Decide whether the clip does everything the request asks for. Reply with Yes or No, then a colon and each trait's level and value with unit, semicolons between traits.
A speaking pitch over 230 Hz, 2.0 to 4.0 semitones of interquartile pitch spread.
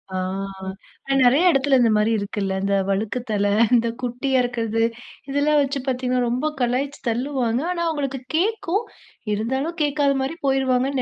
Yes: very high, 260 Hz; average, 3.3 semitones